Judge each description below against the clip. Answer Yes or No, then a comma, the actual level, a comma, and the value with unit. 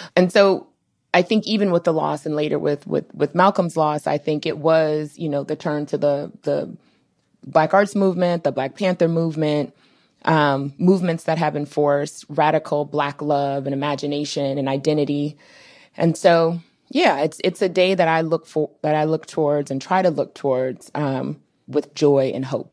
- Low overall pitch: No, medium, 150 Hz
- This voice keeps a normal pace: Yes, average, 185 wpm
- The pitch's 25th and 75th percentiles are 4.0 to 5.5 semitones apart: No, average, 2.7 semitones